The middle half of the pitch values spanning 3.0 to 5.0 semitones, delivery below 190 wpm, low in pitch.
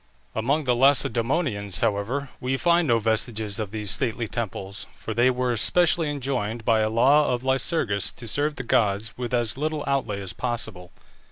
Yes: average, 4.0 semitones; average, 170 wpm; low, 120 Hz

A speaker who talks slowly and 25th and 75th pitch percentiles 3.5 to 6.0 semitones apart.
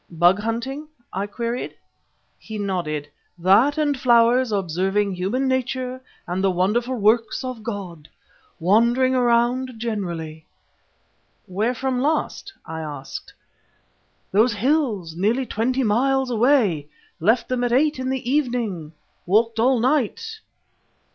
Yes: slow, 120 wpm; average, 5.1 semitones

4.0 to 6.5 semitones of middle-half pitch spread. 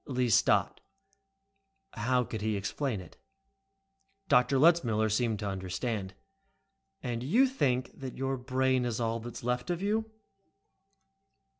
No: average, 3.3 semitones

